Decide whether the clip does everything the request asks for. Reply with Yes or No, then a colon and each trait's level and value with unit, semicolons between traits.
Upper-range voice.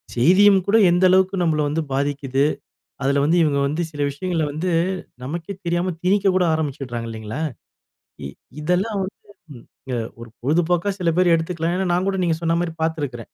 No: medium, 165 Hz